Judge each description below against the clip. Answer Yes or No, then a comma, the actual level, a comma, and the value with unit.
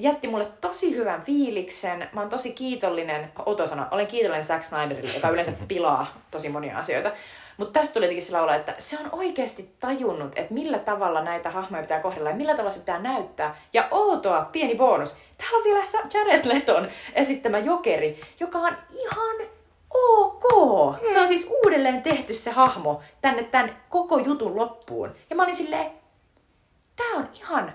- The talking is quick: Yes, fast, 165 wpm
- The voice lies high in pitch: Yes, very high, 260 Hz